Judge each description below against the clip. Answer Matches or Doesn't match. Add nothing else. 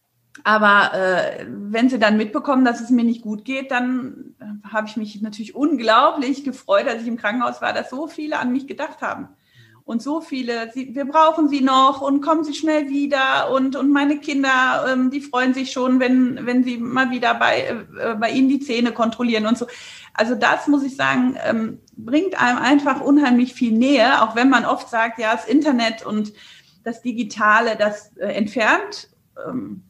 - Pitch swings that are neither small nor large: Matches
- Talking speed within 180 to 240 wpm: Matches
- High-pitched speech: Matches